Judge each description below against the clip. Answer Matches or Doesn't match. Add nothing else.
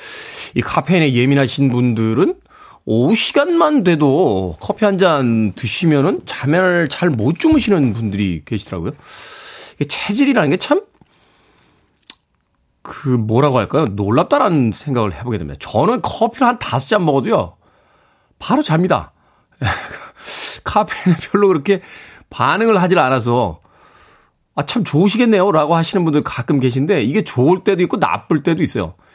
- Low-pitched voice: Doesn't match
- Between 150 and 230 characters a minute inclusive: Doesn't match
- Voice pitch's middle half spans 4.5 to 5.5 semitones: Doesn't match